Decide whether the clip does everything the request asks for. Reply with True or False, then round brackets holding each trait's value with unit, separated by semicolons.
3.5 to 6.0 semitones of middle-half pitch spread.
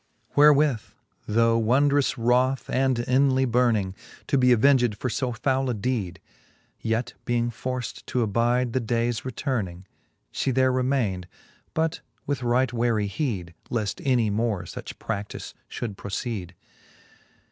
False (2.9 semitones)